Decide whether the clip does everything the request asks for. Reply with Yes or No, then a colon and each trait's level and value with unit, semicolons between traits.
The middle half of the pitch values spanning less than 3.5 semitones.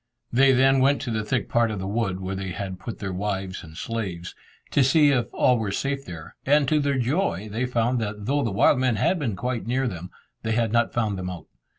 No: average, 5.2 semitones